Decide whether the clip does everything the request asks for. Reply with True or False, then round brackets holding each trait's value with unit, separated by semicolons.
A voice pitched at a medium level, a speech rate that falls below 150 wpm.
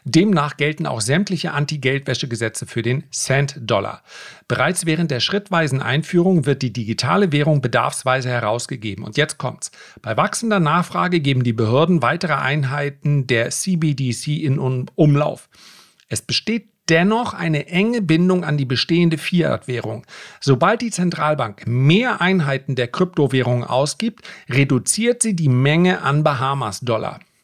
True (145 Hz; 125 wpm)